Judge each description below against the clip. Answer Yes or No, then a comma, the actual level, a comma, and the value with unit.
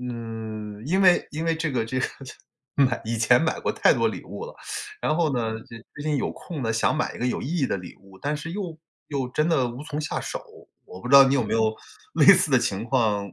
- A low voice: Yes, low, 130 Hz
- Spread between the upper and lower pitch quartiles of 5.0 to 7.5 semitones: Yes, wide, 5.5 semitones